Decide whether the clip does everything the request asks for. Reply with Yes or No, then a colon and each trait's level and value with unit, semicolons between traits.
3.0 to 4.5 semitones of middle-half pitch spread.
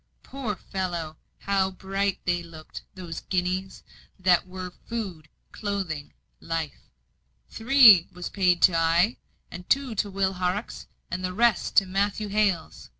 No: narrow, 2.4 semitones